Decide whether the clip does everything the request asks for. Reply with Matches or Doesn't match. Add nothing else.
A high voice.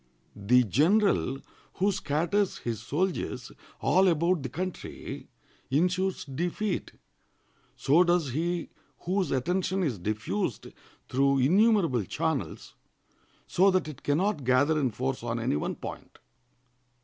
Doesn't match